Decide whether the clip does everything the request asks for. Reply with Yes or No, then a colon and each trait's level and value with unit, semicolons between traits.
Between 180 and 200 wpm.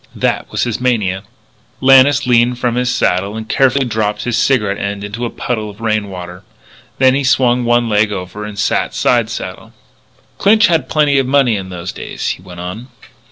Yes: average, 190 wpm